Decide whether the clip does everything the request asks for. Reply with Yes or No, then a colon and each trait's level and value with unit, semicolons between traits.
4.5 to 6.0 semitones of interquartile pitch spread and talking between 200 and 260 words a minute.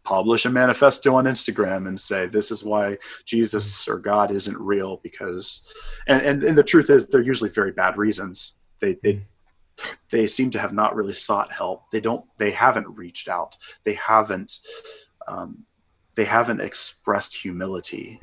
No: wide, 5.5 semitones; average, 165 wpm